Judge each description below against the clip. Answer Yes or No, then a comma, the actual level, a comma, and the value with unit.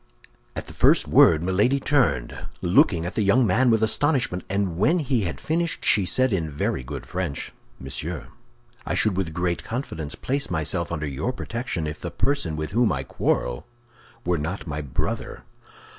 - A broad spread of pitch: Yes, wide, 7.6 semitones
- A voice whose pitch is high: No, very low, 90 Hz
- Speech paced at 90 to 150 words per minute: No, average, 175 wpm